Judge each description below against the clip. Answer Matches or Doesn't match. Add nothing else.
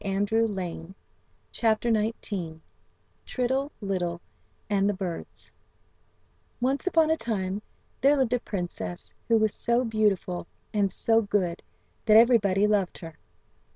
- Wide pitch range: Doesn't match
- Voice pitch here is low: Doesn't match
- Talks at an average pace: Doesn't match